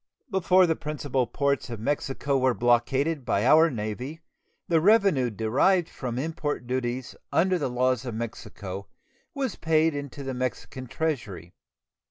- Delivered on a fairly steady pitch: No, average, 4.8 semitones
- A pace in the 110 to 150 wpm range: Yes, average, 140 wpm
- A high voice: No, low, 135 Hz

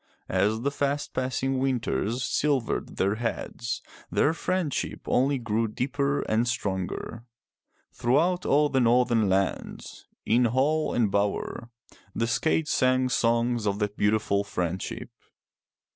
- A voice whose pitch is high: No, low, 120 Hz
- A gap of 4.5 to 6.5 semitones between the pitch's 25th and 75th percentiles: No, average, 3.9 semitones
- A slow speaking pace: Yes, slow, 120 wpm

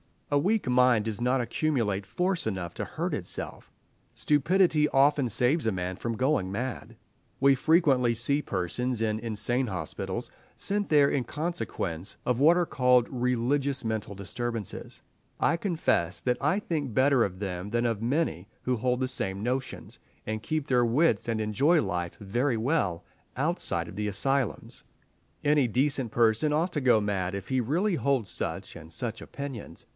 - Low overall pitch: Yes, low, 125 Hz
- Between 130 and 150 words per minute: No, average, 160 wpm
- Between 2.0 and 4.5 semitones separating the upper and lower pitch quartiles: No, average, 5.2 semitones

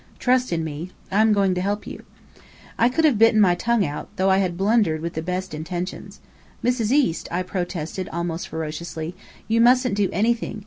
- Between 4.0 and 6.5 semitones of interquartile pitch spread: Yes, average, 4.9 semitones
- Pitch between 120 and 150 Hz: No, high, 190 Hz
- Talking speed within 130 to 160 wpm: No, average, 185 wpm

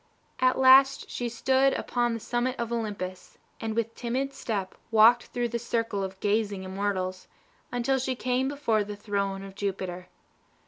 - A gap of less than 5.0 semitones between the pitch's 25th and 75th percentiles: Yes, average, 3.7 semitones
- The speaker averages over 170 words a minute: No, average, 155 wpm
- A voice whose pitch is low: No, high, 230 Hz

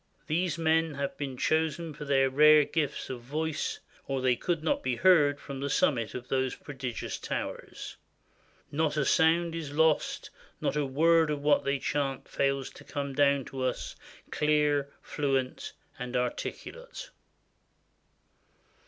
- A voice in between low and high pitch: Yes, medium, 145 Hz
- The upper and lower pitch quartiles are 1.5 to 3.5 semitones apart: Yes, average, 2.9 semitones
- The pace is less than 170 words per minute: Yes, average, 150 wpm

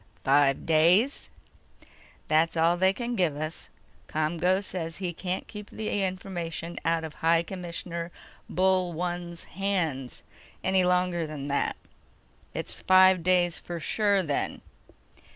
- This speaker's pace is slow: Yes, slow, 120 wpm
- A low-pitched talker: No, medium, 175 Hz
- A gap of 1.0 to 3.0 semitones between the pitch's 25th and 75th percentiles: Yes, narrow, 2.4 semitones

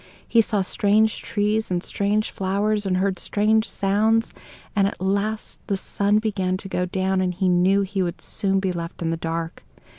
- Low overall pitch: No, high, 195 Hz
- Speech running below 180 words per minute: No, average, 185 wpm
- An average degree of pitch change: No, narrow, 2.1 semitones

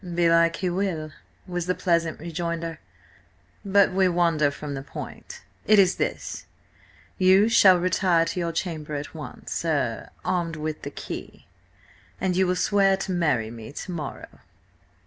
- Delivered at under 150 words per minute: Yes, average, 140 wpm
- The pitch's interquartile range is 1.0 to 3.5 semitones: Yes, average, 3.1 semitones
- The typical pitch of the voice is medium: Yes, medium, 170 Hz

